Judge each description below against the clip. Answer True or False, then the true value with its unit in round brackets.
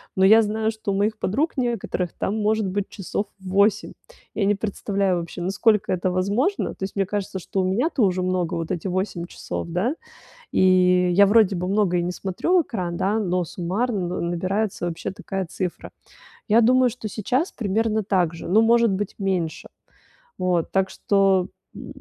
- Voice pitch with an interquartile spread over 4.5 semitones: False (3.0 semitones)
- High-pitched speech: True (195 Hz)